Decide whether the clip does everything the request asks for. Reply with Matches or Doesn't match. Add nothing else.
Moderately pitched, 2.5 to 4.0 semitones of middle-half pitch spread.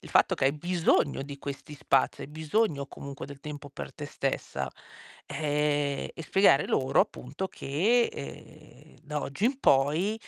Matches